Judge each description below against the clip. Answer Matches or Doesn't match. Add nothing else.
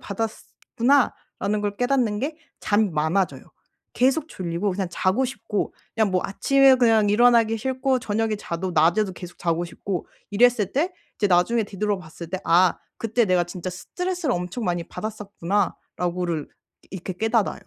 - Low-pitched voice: Doesn't match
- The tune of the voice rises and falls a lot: Doesn't match